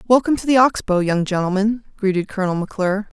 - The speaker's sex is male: No, female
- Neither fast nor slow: Yes, average, 190 wpm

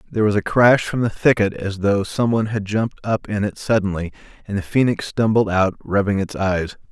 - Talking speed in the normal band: No, fast, 210 wpm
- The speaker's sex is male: Yes, male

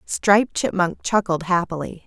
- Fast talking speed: No, slow, 115 wpm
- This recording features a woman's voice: Yes, female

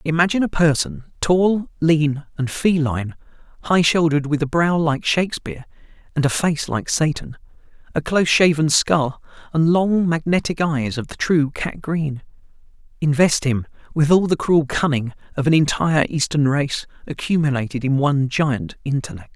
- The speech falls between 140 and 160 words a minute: Yes, average, 150 wpm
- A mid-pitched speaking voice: Yes, medium, 155 Hz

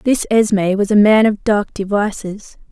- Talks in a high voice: Yes, high, 205 Hz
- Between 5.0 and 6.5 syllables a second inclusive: No, 4.8 syllables/s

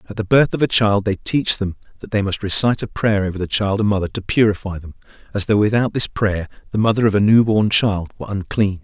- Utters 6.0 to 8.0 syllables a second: Yes, 6.1 syllables/s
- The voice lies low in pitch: Yes, low, 105 Hz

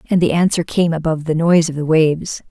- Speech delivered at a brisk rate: Yes, fast, 240 wpm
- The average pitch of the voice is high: No, medium, 165 Hz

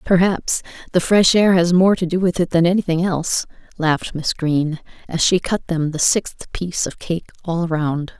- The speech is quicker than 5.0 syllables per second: No, 4.9 syllables/s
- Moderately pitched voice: Yes, medium, 170 Hz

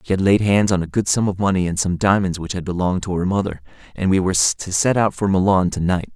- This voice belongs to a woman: No, male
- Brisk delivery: Yes, fast, 285 wpm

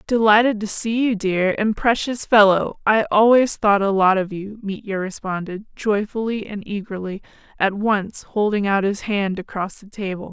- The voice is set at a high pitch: Yes, high, 205 Hz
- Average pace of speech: Yes, average, 170 wpm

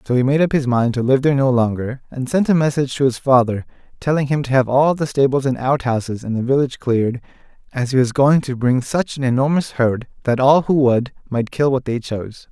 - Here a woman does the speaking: No, male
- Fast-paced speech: Yes, fast, 240 wpm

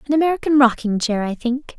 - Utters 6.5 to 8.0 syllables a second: No, 6.1 syllables/s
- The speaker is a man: No, female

